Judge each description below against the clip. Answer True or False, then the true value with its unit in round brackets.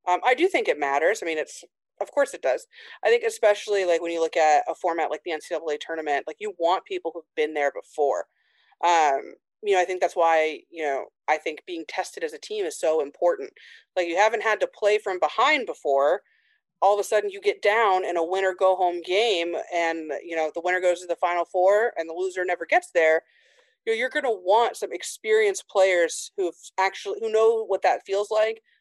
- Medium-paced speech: False (230 wpm)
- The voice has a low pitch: False (195 Hz)